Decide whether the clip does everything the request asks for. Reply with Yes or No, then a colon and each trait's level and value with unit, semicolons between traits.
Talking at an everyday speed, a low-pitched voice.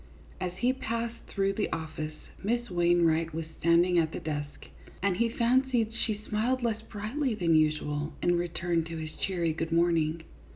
No: average, 165 wpm; medium, 175 Hz